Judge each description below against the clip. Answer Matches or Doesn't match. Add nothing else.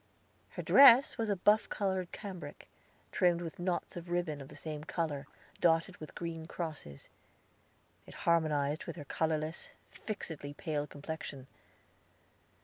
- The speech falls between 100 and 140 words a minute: Matches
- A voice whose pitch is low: Doesn't match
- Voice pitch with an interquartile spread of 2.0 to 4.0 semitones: Matches